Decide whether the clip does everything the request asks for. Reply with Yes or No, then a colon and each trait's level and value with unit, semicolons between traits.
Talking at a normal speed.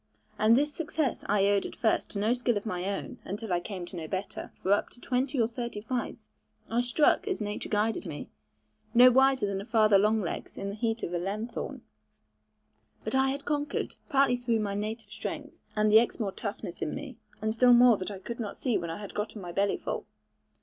No: fast, 215 wpm